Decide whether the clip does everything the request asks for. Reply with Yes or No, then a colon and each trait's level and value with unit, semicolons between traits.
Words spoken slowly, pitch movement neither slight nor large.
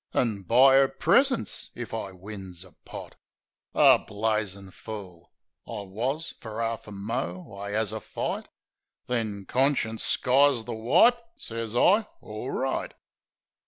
Yes: slow, 130 wpm; average, 3.8 semitones